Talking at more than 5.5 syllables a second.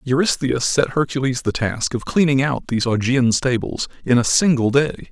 No: 5.1 syllables/s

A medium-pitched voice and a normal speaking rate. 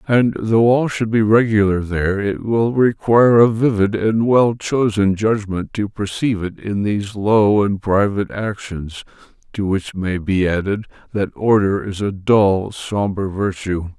No: low, 105 Hz; average, 160 wpm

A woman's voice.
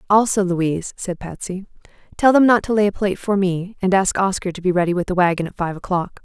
Yes: female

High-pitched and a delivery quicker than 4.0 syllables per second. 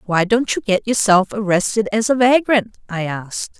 Yes: high, 210 Hz; 5.0 syllables/s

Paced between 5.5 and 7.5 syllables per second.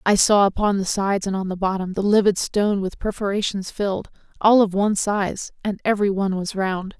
Yes: 5.8 syllables/s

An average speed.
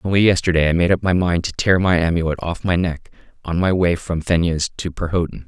No: fast, 240 wpm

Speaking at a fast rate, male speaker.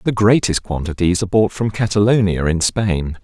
No: average, 165 wpm; male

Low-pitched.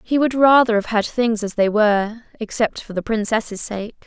No: high, 220 Hz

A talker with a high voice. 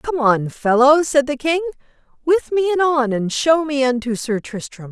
Yes: very high, 275 Hz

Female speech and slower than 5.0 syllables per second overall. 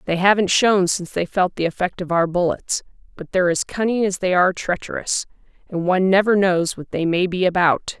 No: female; 5.6 syllables/s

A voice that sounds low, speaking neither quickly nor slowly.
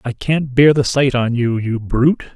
No: low, 130 Hz; fast, 230 wpm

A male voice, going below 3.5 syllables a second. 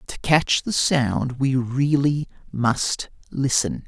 Yes: male; 3.0 syllables/s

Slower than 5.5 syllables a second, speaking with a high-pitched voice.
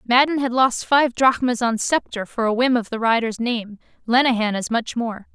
Yes: 4.9 syllables/s; high, 240 Hz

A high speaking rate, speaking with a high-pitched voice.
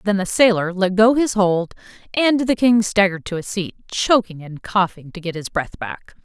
Yes: fast, 210 wpm; high, 195 Hz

